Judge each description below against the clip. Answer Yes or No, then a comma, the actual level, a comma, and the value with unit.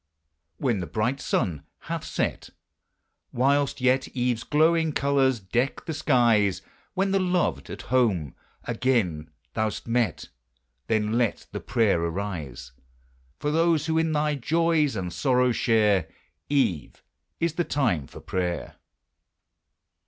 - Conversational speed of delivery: No, slow, 130 wpm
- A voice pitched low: Yes, low, 125 Hz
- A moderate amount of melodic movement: No, wide, 6.6 semitones